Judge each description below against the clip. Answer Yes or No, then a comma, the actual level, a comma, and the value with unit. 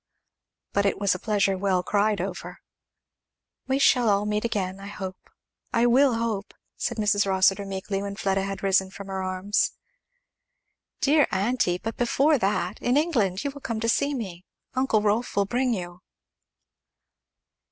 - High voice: Yes, high, 205 Hz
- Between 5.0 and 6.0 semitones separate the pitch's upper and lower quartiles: No, average, 3.5 semitones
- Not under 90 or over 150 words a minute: No, average, 165 wpm